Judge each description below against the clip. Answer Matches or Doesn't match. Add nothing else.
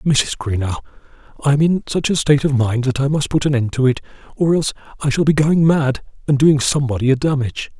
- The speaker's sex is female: Doesn't match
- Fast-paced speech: Matches